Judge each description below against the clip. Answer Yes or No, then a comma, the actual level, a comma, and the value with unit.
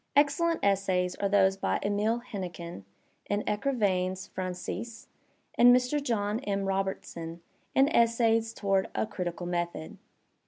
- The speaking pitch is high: Yes, high, 200 Hz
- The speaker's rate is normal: No, slow, 120 wpm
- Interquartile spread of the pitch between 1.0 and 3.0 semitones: No, average, 4.0 semitones